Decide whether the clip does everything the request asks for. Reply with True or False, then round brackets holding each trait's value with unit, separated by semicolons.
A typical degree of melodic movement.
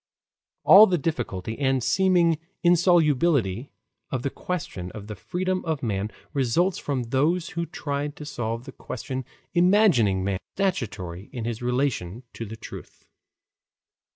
False (7.3 semitones)